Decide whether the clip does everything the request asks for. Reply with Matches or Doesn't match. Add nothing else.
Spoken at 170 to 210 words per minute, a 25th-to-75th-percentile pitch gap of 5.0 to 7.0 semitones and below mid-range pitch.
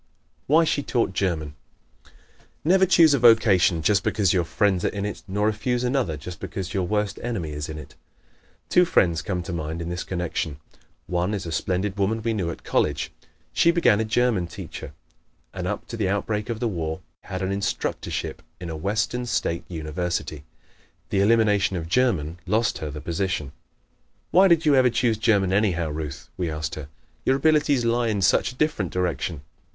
Matches